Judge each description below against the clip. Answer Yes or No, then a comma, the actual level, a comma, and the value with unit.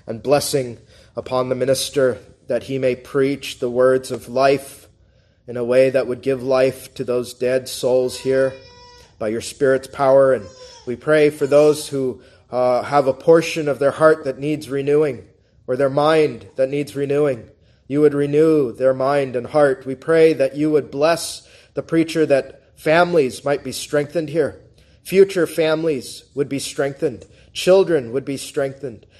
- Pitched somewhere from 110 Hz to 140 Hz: Yes, low, 135 Hz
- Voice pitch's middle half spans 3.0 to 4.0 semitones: No, narrow, 2.6 semitones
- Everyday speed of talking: Yes, average, 165 wpm